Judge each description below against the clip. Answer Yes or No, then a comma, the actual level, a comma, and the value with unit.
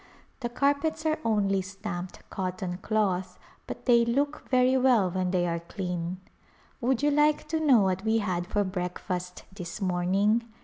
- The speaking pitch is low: No, high, 200 Hz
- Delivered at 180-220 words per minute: No, average, 160 wpm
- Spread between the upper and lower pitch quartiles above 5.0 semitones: Yes, wide, 5.6 semitones